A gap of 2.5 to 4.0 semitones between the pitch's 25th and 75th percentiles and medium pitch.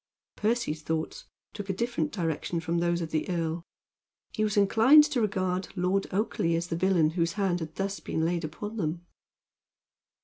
Yes: average, 3.7 semitones; medium, 175 Hz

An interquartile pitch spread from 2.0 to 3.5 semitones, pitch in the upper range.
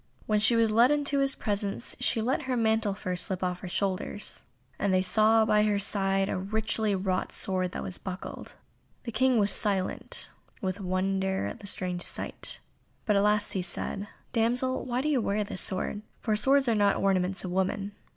Yes: average, 2.8 semitones; high, 205 Hz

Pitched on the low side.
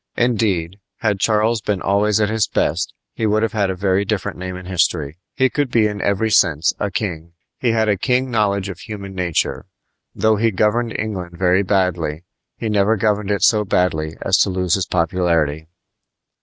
Yes: low, 100 Hz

